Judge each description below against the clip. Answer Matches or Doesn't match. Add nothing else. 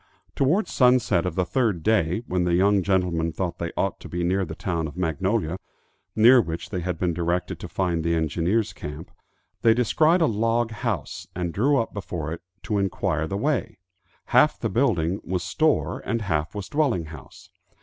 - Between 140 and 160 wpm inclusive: Doesn't match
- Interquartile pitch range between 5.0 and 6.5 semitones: Matches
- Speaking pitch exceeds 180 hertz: Doesn't match